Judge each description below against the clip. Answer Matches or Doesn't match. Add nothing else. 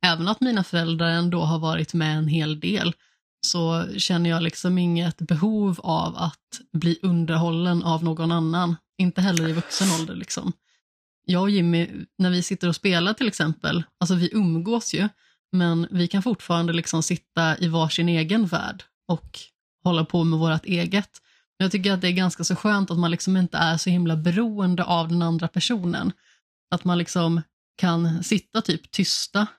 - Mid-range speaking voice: Matches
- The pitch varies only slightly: Matches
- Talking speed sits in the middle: Matches